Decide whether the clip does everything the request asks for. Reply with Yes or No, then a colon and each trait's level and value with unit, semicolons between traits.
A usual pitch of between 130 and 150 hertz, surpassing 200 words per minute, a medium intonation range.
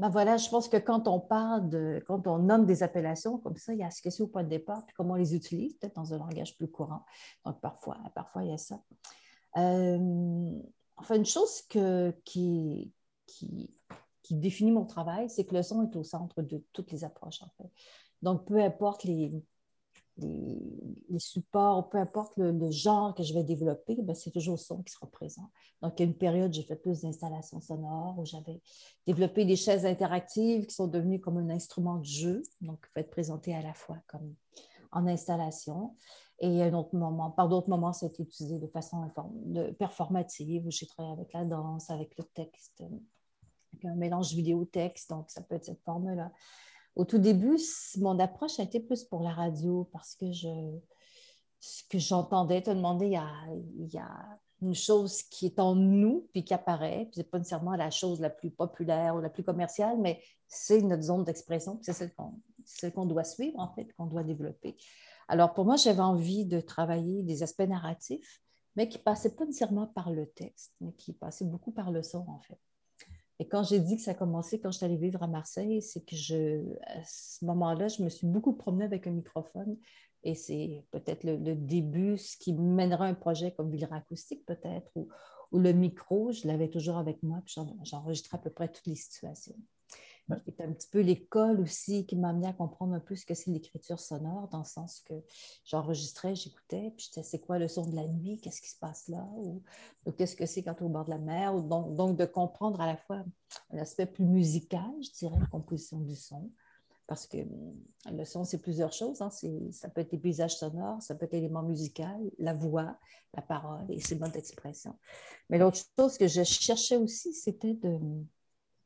No: medium, 175 Hz; average, 210 wpm; average, 3.4 semitones